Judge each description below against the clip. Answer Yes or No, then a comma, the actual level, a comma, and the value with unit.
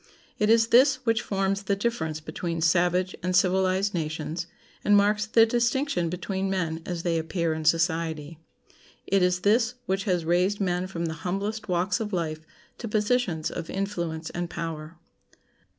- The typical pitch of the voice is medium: Yes, medium, 180 Hz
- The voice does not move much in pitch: No, average, 3.6 semitones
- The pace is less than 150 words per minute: No, average, 160 wpm